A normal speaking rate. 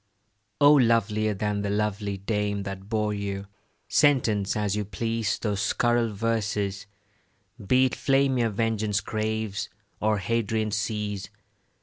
No: slow, 125 wpm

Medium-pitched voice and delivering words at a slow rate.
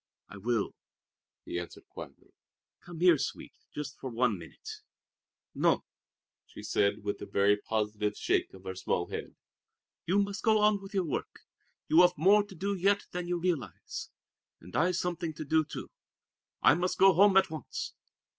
No: medium, 165 Hz; average, 170 wpm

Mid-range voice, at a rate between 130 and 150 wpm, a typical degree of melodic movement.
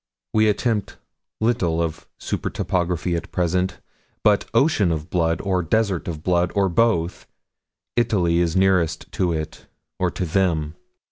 No: very low, 90 Hz; average, 140 wpm; average, 3.2 semitones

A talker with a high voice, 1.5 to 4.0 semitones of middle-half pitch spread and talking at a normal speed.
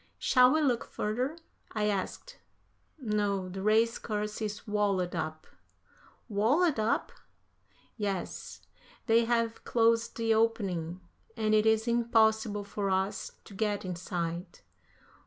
No: high, 215 Hz; narrow, 2.6 semitones; slow, 120 wpm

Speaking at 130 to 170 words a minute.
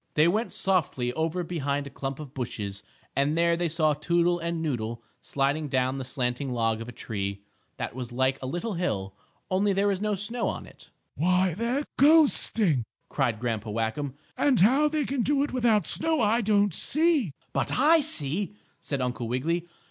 No: average, 180 wpm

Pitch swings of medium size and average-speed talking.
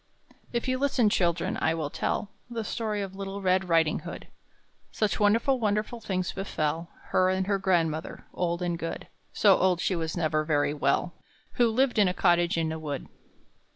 Yes: average, 4.0 semitones; average, 180 wpm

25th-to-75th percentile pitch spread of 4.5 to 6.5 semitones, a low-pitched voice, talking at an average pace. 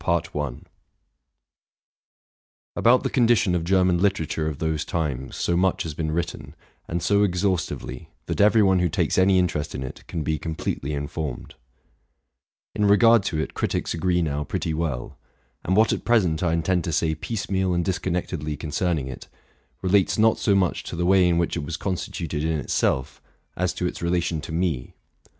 No: average, 3.3 semitones; very low, 85 Hz; average, 170 wpm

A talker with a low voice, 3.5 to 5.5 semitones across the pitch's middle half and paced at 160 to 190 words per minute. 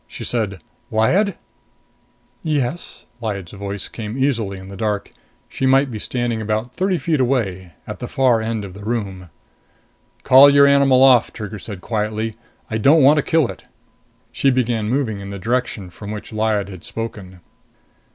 Yes: low, 110 Hz; average, 4.6 semitones; average, 165 wpm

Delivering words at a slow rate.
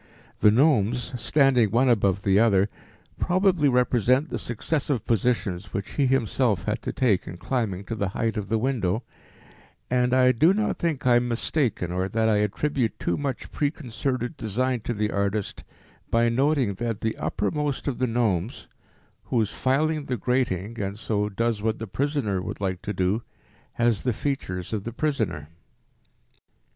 No: average, 165 wpm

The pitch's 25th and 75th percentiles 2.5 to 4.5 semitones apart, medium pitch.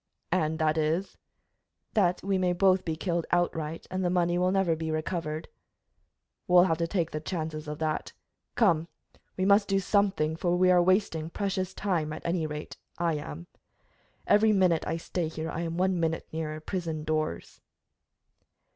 Yes: average, 2.9 semitones; medium, 170 Hz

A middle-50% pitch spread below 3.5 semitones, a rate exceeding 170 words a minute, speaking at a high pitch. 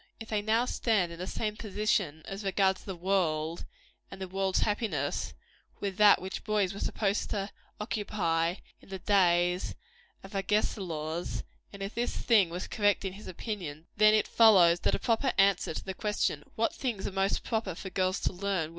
Yes: average, 2.9 semitones; average, 180 wpm; high, 195 Hz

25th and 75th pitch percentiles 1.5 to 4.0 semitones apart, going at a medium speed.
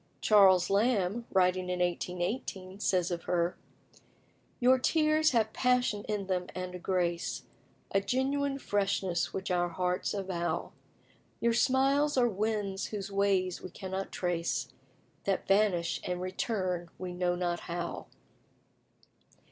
No: average, 3.3 semitones; slow, 125 wpm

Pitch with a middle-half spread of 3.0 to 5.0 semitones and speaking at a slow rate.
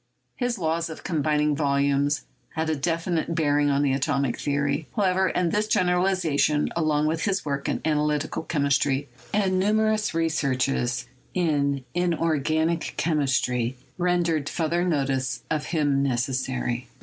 Yes: average, 3.4 semitones; slow, 125 wpm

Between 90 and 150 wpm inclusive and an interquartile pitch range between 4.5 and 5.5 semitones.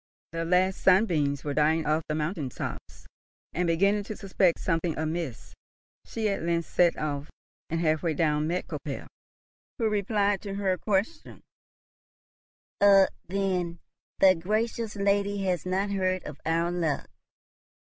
No: average, 140 wpm; average, 3.5 semitones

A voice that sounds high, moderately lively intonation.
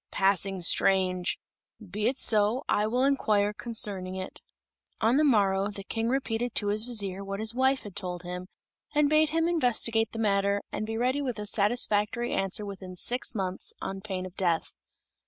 Yes: high, 210 Hz; average, 3.8 semitones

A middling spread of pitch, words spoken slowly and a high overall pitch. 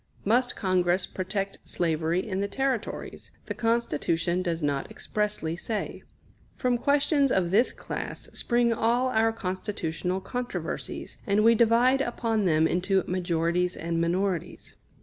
Yes: average, 4.9 semitones; slow, 130 wpm; high, 195 Hz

